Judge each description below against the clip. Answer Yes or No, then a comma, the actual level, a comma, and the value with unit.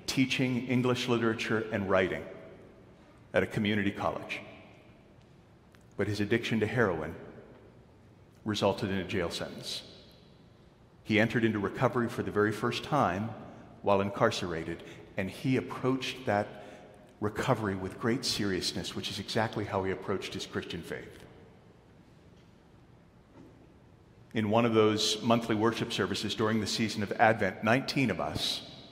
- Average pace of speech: No, slow, 130 wpm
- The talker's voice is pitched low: Yes, low, 110 Hz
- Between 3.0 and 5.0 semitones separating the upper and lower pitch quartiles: No, narrow, 2.6 semitones